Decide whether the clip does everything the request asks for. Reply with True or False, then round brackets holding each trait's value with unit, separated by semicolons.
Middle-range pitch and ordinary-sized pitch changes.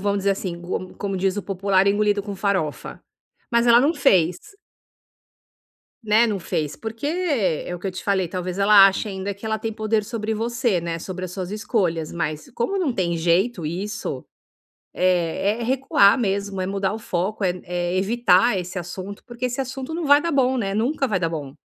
False (200 Hz; 3.7 semitones)